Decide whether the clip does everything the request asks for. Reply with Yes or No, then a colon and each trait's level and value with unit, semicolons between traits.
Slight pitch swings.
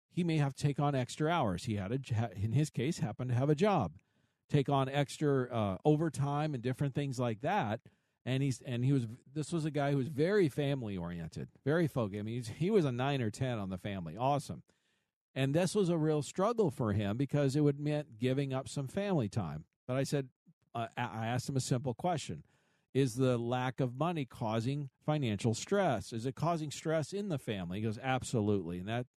No: average, 4.1 semitones